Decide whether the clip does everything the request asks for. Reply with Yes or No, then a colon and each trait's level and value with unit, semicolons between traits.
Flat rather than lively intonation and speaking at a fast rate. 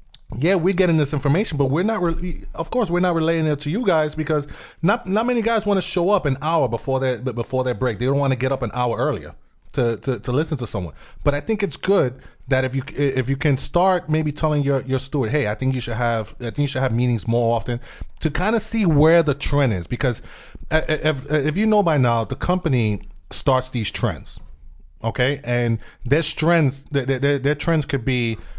No: average, 4.9 semitones; fast, 230 wpm